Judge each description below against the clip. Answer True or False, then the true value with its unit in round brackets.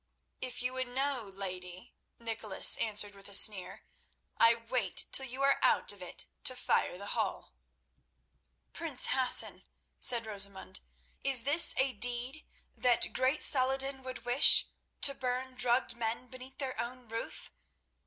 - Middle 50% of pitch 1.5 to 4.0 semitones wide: True (3.5 semitones)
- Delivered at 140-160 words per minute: True (145 wpm)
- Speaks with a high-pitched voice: True (245 Hz)